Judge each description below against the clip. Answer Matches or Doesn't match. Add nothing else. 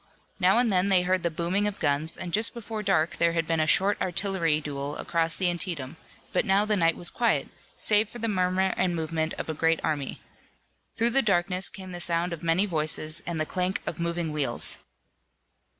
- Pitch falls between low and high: Matches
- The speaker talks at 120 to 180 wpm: Doesn't match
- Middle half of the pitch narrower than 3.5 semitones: Matches